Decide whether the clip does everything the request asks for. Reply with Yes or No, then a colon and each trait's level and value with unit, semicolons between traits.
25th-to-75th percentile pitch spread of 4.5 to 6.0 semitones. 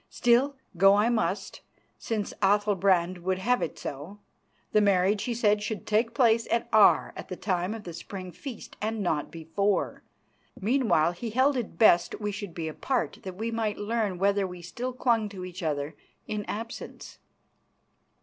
No: average, 3.9 semitones